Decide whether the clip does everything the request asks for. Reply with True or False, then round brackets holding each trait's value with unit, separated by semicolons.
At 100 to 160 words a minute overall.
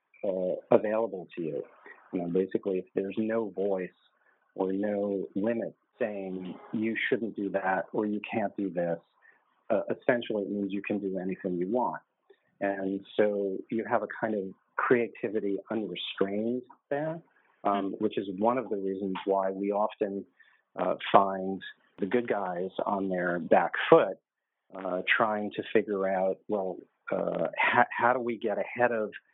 True (155 wpm)